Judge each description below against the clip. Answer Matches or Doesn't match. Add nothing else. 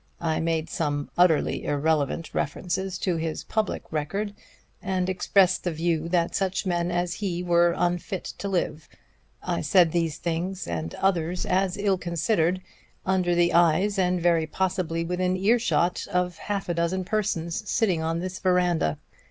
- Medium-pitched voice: Matches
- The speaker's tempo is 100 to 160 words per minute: Matches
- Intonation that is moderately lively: Doesn't match